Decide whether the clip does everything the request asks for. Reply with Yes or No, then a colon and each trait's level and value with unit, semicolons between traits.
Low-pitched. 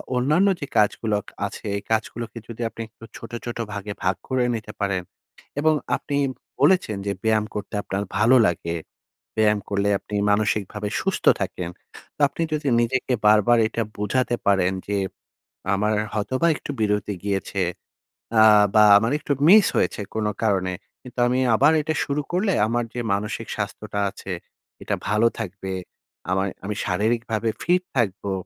Yes: low, 110 Hz